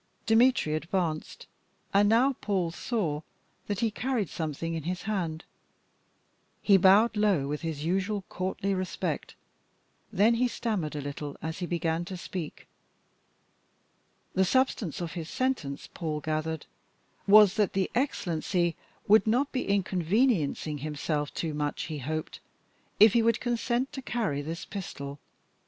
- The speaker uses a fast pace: No, average, 140 wpm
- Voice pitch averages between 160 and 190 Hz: Yes, medium, 185 Hz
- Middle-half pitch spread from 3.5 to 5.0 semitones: No, wide, 5.4 semitones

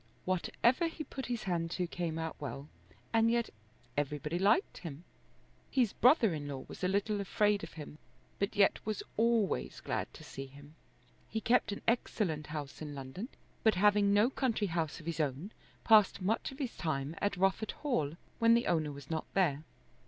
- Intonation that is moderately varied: No, wide, 6.5 semitones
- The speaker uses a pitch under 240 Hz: Yes, high, 190 Hz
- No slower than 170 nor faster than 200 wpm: Yes, average, 180 wpm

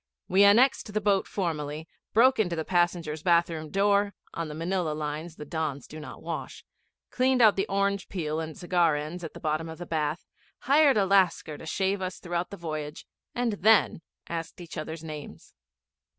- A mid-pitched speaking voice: Yes, medium, 170 Hz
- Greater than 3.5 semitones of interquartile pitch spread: Yes, average, 4.1 semitones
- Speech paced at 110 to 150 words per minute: No, average, 185 wpm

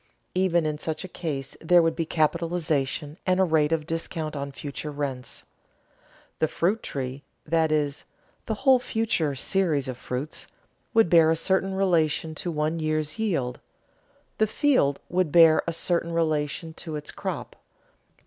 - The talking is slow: No, average, 155 wpm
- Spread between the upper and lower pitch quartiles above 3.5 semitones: No, average, 2.8 semitones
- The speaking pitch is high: No, medium, 160 Hz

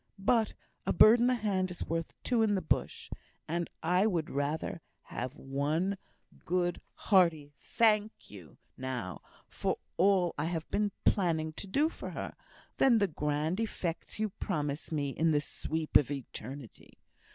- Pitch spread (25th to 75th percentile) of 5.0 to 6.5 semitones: Yes, wide, 5.5 semitones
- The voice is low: No, medium, 170 Hz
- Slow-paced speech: No, average, 160 wpm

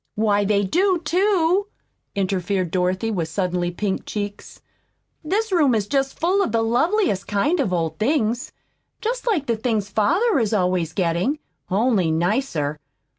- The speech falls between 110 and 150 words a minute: Yes, average, 145 wpm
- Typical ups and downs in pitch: No, wide, 8.8 semitones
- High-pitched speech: Yes, high, 215 Hz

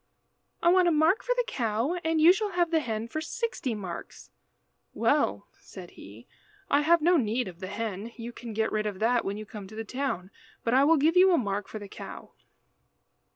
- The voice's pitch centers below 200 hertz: No, high, 235 Hz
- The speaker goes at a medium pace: No, fast, 215 wpm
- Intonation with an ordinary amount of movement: No, wide, 7.7 semitones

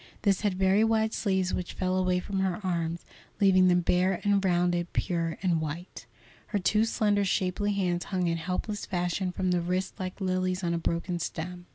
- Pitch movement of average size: No, narrow, 1.7 semitones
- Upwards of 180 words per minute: Yes, average, 190 wpm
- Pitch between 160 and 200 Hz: Yes, medium, 185 Hz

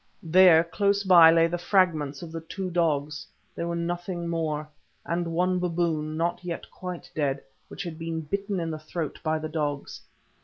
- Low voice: No, medium, 165 Hz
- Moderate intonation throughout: No, narrow, 2.1 semitones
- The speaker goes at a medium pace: Yes, average, 165 wpm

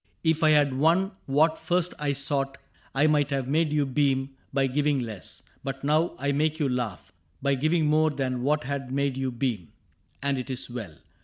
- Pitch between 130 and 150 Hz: Yes, medium, 140 Hz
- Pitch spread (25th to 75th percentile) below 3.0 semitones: Yes, narrow, 2.5 semitones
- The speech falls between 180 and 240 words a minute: Yes, average, 190 wpm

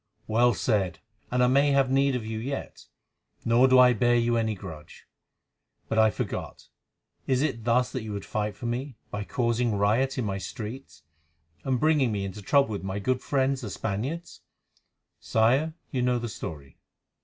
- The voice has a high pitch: No, low, 120 Hz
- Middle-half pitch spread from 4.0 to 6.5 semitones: No, average, 3.6 semitones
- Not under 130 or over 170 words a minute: No, average, 180 wpm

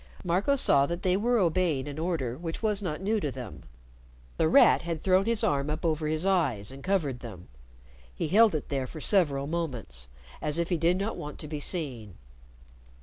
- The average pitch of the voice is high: No, medium, 160 Hz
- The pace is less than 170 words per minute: No, average, 200 wpm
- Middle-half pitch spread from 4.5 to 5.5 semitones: Yes, average, 5.0 semitones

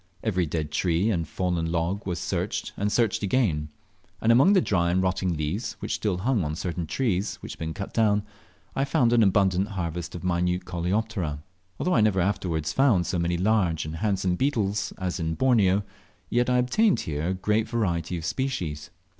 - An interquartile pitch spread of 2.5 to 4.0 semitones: No, average, 4.4 semitones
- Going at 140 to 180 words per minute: No, average, 190 wpm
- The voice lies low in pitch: Yes, very low, 95 Hz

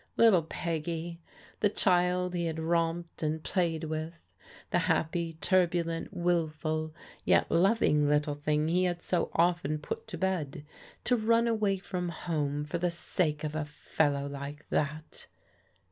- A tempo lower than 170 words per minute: Yes, average, 145 wpm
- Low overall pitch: No, medium, 165 Hz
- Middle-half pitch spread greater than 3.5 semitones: No, narrow, 2.6 semitones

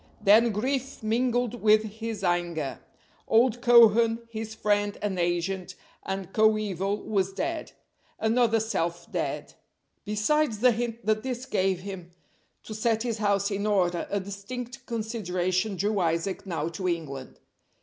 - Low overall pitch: No, high, 210 Hz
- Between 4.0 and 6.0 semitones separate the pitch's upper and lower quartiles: No, average, 3.3 semitones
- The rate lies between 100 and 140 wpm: Yes, slow, 135 wpm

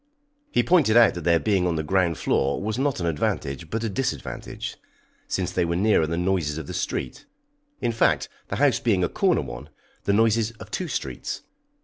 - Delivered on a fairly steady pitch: No, wide, 5.5 semitones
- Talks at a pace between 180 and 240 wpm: Yes, average, 200 wpm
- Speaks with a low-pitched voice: Yes, very low, 95 Hz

